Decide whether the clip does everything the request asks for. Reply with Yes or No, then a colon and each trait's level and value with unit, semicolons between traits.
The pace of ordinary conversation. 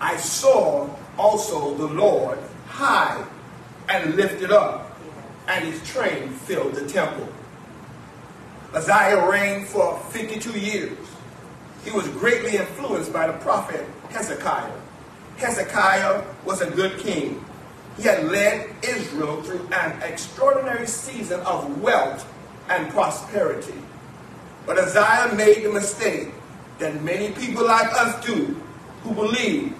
No: slow, 115 wpm